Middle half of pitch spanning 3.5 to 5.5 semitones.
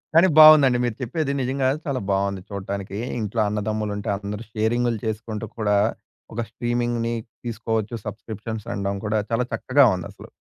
No: average, 2.8 semitones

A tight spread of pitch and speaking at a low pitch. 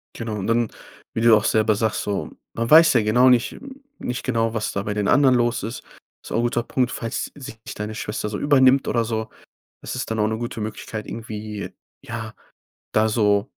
Yes: narrow, 2.0 semitones; low, 115 Hz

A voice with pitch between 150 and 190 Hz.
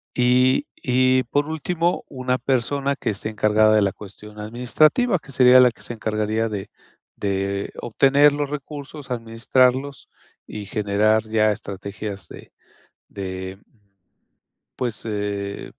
No: low, 115 Hz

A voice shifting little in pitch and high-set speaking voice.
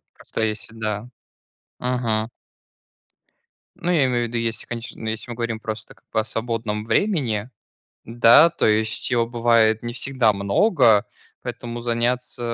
No: narrow, 1.9 semitones; low, 115 Hz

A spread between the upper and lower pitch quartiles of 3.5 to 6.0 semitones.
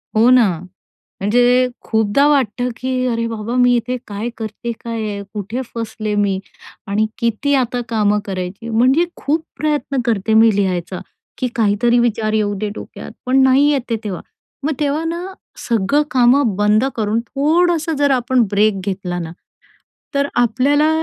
Yes: average, 4.1 semitones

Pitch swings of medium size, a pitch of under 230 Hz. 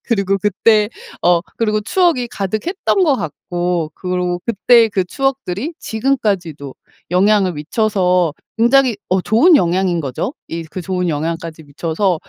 Yes: average, 4.7 semitones; high, 190 Hz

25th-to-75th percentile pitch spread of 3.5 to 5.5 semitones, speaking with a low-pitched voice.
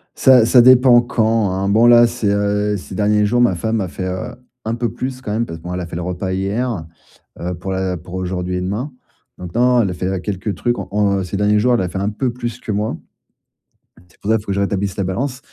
Yes: average, 4.2 semitones; low, 105 Hz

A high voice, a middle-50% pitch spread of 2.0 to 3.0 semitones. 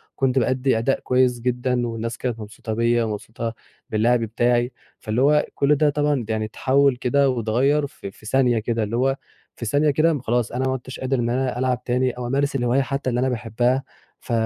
No: low, 125 Hz; narrow, 2.4 semitones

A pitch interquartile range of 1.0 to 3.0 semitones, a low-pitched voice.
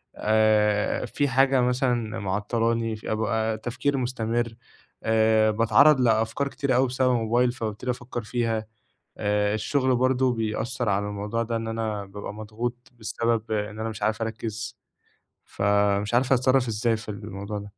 Yes: narrow, 2.4 semitones; low, 115 Hz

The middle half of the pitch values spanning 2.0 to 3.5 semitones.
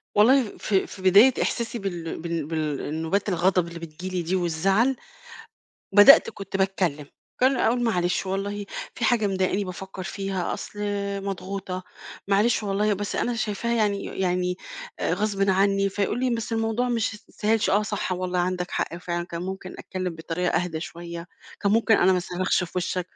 Yes: average, 2.8 semitones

